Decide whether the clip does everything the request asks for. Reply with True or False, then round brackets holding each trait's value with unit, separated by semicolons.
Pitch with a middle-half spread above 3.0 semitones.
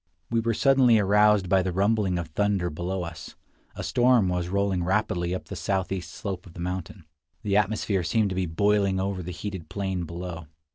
False (2.6 semitones)